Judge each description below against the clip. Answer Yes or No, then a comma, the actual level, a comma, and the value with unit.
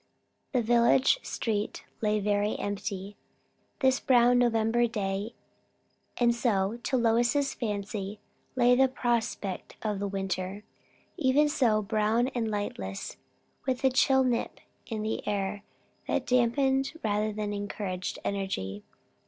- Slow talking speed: Yes, slow, 120 wpm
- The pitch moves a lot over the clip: No, average, 3.2 semitones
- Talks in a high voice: Yes, high, 220 Hz